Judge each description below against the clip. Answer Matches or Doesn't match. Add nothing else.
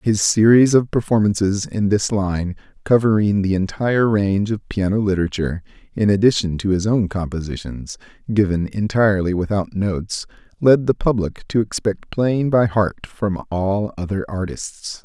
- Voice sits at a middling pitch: Doesn't match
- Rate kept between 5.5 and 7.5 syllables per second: Doesn't match